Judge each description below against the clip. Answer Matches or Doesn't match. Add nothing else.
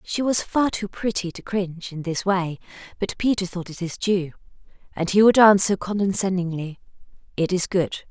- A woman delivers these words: Matches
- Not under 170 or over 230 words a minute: Matches